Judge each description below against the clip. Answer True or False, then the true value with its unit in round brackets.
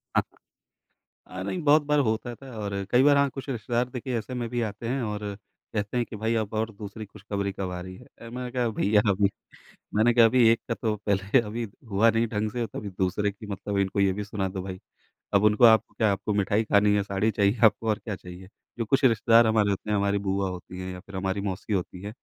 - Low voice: True (105 Hz)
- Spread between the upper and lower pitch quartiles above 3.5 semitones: False (2.7 semitones)